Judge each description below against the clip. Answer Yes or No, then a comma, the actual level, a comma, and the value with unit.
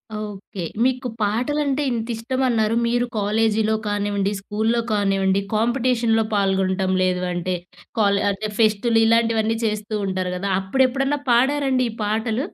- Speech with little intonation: No, average, 3.1 semitones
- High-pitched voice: Yes, high, 220 Hz